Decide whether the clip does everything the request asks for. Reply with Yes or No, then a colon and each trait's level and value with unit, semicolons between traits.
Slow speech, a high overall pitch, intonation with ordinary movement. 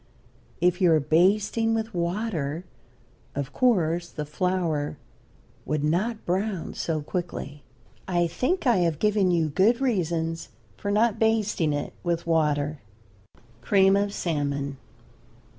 No: slow, 125 wpm; medium, 175 Hz; average, 4.9 semitones